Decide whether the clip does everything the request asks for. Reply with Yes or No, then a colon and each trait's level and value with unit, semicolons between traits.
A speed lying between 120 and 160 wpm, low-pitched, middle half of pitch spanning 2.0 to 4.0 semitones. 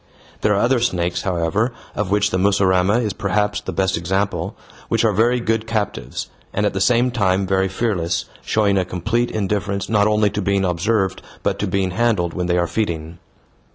No: average, 190 wpm; low, 100 Hz; average, 2.9 semitones